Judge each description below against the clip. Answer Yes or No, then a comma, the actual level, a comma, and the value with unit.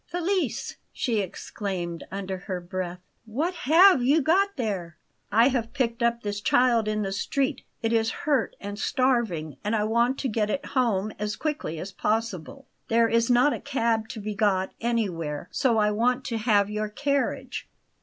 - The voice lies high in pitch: Yes, high, 225 Hz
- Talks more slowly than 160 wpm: No, average, 175 wpm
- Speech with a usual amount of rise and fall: Yes, average, 3.9 semitones